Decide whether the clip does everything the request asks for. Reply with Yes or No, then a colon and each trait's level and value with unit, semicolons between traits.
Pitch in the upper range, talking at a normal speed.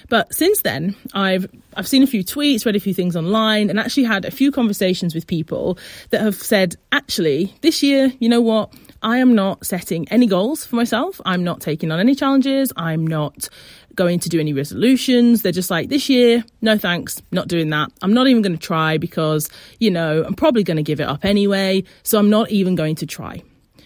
No: high, 200 Hz; fast, 215 wpm